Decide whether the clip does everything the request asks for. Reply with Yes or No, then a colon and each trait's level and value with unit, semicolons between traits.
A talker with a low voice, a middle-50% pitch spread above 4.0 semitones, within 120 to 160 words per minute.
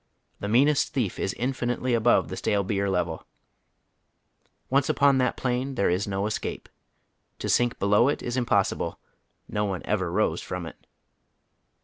Yes: low, 110 Hz; average, 4.5 semitones; average, 150 wpm